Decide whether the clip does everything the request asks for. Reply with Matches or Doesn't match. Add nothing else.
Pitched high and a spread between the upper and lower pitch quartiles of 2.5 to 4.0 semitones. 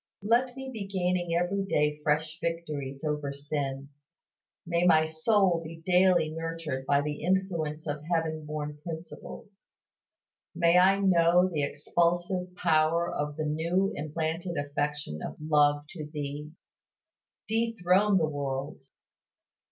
Doesn't match